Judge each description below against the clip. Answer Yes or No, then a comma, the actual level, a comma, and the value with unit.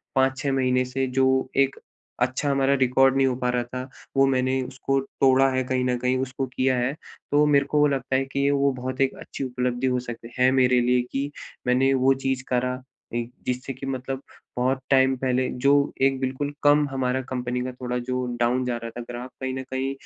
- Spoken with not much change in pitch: Yes, narrow, 1.1 semitones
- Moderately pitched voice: No, low, 130 Hz